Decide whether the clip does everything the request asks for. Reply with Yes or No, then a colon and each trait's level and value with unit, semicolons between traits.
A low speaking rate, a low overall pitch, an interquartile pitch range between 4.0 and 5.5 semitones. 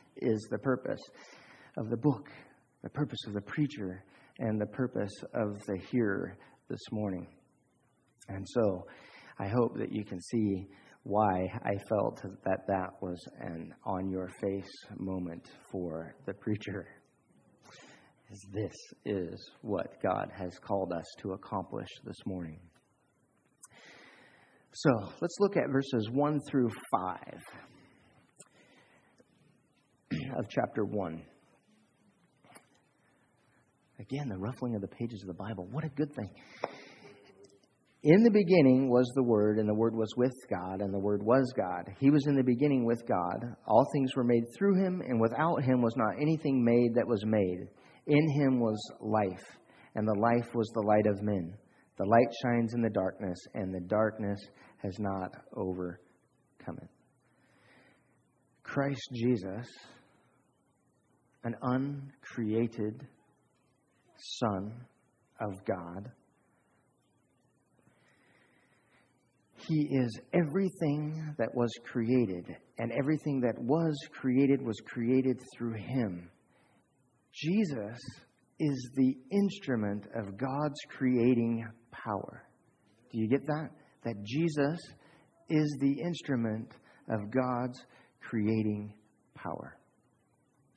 Yes: slow, 120 wpm; low, 120 Hz; average, 4.7 semitones